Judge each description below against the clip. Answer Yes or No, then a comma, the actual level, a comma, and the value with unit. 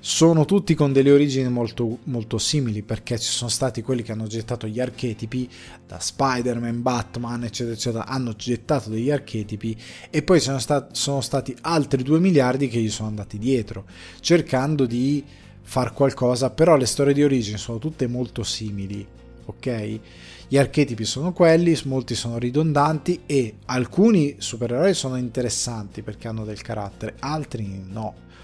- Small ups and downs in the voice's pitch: No, average, 4.0 semitones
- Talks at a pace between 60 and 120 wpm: No, average, 155 wpm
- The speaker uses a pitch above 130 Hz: No, low, 125 Hz